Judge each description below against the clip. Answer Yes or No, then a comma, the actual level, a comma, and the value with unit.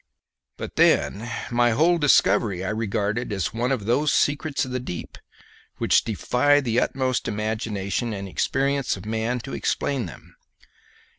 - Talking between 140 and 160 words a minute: Yes, average, 145 wpm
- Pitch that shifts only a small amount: No, average, 4.2 semitones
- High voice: No, low, 120 Hz